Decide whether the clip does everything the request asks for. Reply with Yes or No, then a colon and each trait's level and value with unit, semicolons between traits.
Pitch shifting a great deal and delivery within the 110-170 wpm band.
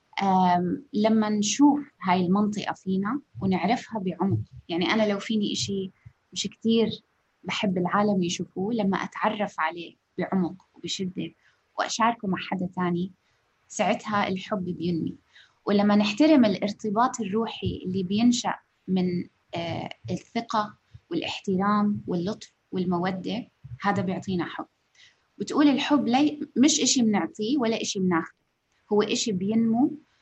No: average, 3.5 semitones; average, 115 wpm